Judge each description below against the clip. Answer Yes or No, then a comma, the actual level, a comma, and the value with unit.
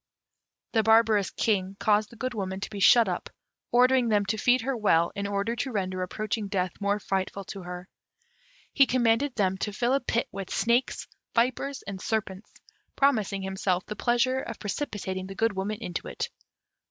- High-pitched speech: Yes, high, 210 Hz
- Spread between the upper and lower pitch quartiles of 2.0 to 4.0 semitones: Yes, average, 3.6 semitones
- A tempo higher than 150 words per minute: Yes, average, 180 wpm